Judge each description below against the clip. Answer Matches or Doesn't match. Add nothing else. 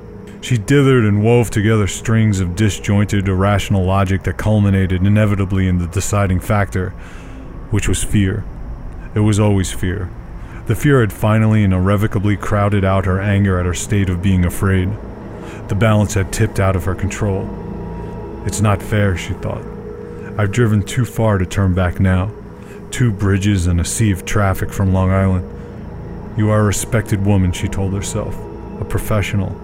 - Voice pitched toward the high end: Doesn't match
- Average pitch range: Doesn't match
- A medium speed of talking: Matches